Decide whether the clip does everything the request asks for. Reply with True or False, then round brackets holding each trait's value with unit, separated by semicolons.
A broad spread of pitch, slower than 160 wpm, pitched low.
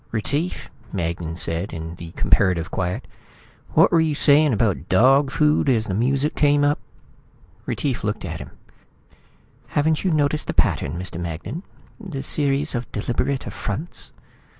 True (8.2 semitones; 145 wpm; 130 Hz)